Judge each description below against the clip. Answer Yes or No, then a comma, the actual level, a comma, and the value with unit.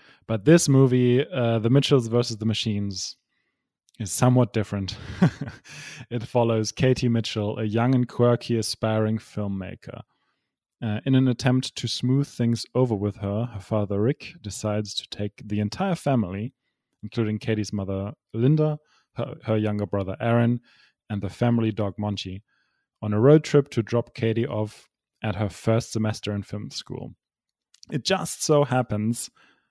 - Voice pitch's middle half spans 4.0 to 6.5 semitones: No, average, 3.3 semitones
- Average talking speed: Yes, average, 150 wpm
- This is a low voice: Yes, low, 115 Hz